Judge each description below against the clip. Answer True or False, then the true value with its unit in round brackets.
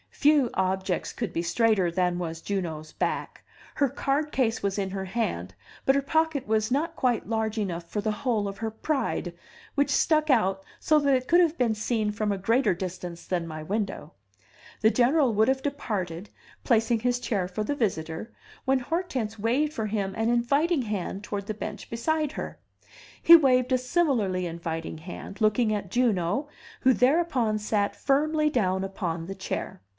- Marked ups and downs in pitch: True (5.7 semitones)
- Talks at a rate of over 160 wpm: True (175 wpm)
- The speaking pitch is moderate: False (220 Hz)